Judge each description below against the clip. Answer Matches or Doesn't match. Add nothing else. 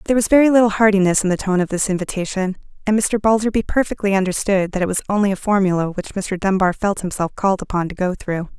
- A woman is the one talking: Matches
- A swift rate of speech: Matches